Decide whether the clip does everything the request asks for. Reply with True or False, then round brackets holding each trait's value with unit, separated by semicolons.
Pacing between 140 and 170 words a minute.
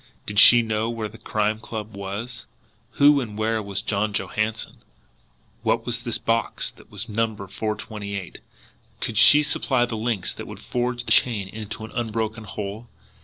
True (165 wpm)